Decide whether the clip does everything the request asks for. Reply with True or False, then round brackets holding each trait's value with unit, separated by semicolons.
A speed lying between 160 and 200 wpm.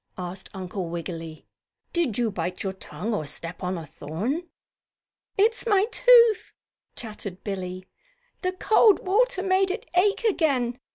False (135 wpm)